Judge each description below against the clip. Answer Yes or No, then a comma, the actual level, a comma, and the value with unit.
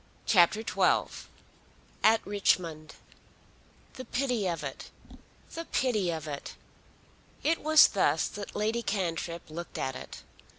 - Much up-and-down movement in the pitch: Yes, wide, 5.7 semitones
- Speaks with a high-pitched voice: Yes, high, 200 Hz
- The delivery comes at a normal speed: No, slow, 120 wpm